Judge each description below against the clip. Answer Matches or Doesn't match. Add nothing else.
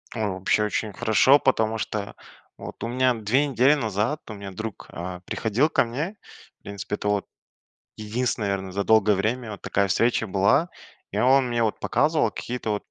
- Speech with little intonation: Doesn't match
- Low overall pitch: Matches